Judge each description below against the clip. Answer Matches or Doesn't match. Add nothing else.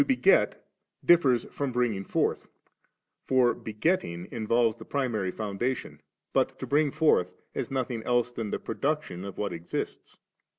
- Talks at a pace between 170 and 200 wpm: Doesn't match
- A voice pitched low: Matches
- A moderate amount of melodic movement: Matches